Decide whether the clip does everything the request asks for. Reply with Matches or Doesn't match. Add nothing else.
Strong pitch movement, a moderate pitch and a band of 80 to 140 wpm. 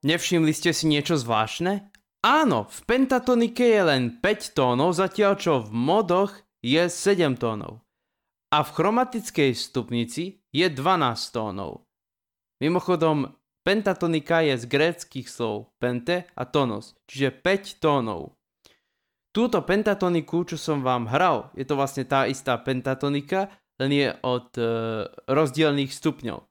Matches